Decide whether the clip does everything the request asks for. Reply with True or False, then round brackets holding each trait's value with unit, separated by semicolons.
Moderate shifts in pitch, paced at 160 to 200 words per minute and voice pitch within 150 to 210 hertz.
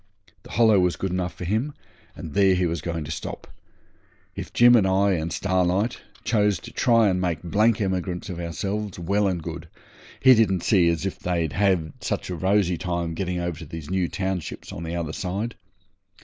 False (3.0 semitones; 190 wpm; 90 Hz)